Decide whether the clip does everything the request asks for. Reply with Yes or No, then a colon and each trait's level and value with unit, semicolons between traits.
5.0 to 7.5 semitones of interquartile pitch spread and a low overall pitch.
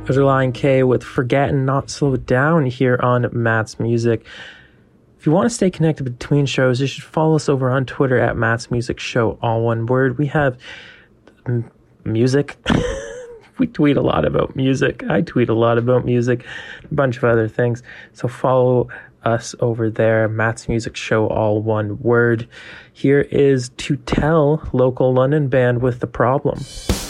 No: average, 3.4 semitones; low, 125 Hz